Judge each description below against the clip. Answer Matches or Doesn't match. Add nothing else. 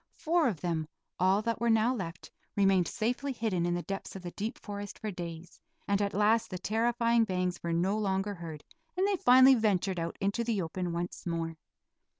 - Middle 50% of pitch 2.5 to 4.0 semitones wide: Doesn't match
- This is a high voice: Matches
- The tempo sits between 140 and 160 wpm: Doesn't match